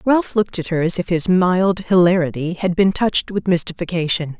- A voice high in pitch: No, medium, 180 Hz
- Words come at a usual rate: Yes, average, 190 wpm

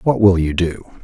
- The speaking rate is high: Yes, fast, 235 wpm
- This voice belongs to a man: Yes, male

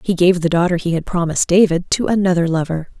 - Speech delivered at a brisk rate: Yes, fast, 220 wpm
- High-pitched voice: No, medium, 175 Hz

